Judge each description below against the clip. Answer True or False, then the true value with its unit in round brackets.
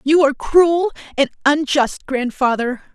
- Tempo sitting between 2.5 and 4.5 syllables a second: True (4.4 syllables/s)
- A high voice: True (285 Hz)